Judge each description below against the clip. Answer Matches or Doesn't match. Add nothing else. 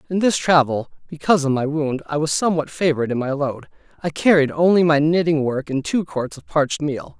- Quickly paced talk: Matches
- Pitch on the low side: Doesn't match